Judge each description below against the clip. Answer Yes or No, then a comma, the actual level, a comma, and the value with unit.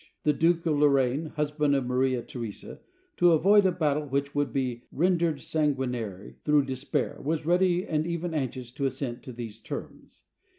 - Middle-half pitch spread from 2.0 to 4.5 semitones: Yes, average, 3.8 semitones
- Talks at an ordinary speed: Yes, average, 170 wpm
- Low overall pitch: No, medium, 145 Hz